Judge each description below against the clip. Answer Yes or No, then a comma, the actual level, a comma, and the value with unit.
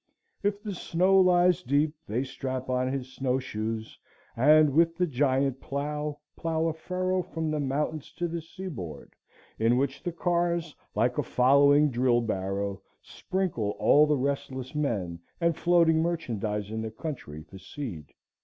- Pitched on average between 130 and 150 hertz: Yes, medium, 140 Hz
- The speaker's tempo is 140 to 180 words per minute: Yes, average, 155 wpm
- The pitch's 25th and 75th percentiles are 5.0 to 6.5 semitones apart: Yes, wide, 5.4 semitones